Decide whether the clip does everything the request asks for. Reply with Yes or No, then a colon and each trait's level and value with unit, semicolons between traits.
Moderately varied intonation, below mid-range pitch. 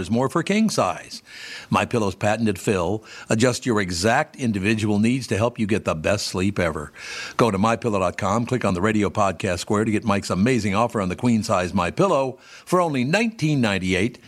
Yes: average, 3.3 semitones; low, 110 Hz